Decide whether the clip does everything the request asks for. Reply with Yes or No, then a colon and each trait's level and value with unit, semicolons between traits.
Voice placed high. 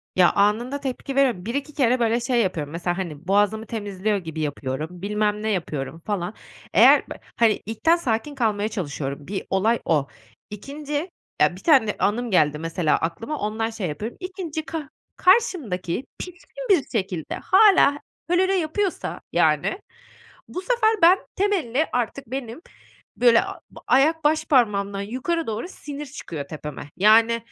Yes: high, 225 Hz